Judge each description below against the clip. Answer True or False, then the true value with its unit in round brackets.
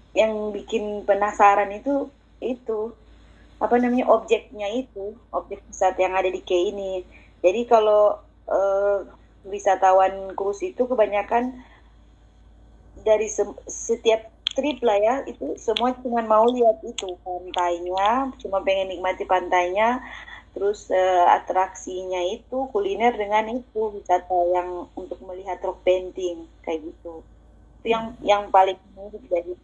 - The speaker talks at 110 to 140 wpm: True (120 wpm)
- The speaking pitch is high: True (200 Hz)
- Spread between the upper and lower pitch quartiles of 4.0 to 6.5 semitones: False (3.4 semitones)